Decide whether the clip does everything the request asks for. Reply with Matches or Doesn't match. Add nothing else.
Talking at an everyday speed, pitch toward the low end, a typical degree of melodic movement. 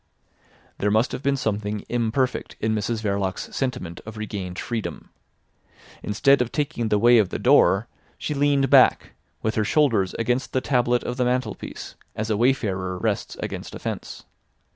Matches